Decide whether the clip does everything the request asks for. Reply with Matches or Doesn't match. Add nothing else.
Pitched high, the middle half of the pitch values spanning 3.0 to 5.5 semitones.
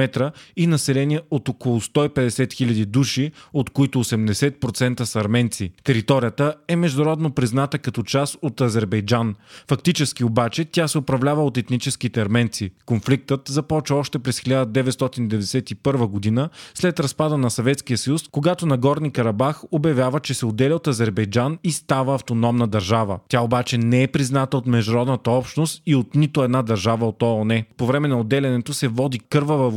Doesn't match